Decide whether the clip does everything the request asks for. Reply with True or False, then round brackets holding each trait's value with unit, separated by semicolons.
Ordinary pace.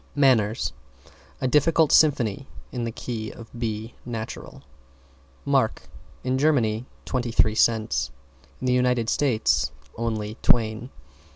False (115 wpm)